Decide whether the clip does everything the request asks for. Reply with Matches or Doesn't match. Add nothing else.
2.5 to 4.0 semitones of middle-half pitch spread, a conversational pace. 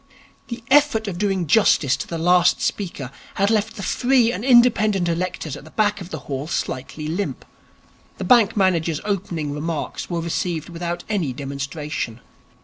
Doesn't match